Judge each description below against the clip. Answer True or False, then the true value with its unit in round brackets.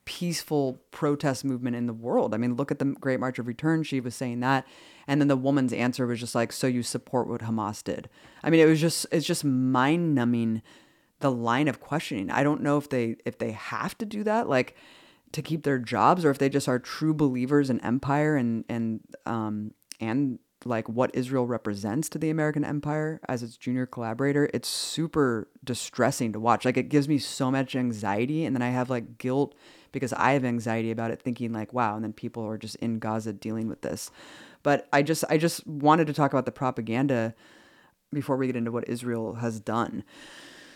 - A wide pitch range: False (3.7 semitones)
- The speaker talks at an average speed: False (210 wpm)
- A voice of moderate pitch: False (130 Hz)